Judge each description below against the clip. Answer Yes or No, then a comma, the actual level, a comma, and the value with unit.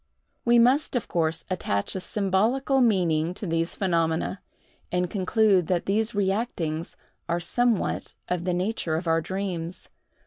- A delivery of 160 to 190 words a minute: No, average, 140 wpm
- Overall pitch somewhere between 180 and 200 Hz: Yes, medium, 185 Hz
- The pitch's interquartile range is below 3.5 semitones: No, average, 4.5 semitones